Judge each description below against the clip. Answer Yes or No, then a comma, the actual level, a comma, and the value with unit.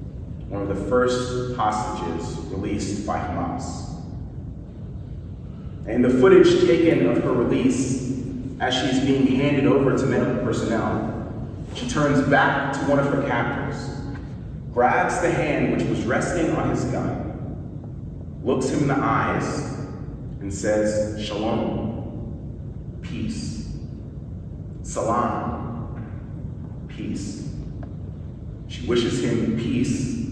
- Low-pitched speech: Yes, low, 125 Hz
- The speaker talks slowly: Yes, slow, 110 wpm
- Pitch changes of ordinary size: Yes, average, 3.4 semitones